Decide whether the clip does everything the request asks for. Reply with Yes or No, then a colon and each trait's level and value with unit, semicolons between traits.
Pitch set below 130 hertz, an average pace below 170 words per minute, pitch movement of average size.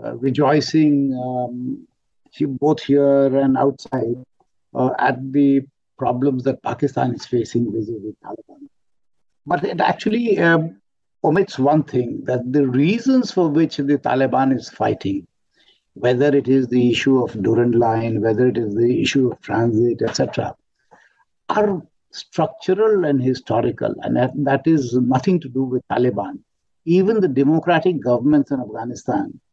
No: low, 135 Hz; average, 140 wpm; average, 3.6 semitones